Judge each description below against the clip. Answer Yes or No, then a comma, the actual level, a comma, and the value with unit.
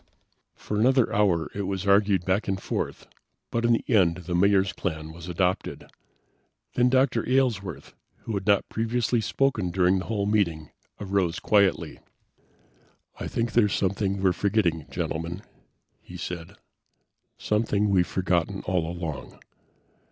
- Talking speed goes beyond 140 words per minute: No, slow, 135 wpm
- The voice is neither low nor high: No, low, 100 Hz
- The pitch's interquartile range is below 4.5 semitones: Yes, average, 3.4 semitones